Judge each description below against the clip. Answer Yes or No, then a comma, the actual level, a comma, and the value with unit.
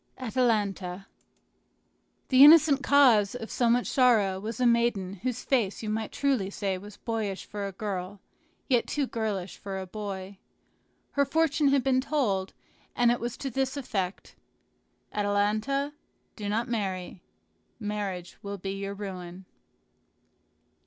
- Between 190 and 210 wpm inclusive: No, average, 140 wpm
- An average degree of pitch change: Yes, average, 4.5 semitones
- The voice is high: Yes, high, 215 Hz